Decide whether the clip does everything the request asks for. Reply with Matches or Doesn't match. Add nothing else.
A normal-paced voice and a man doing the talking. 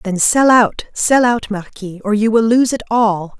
Doesn't match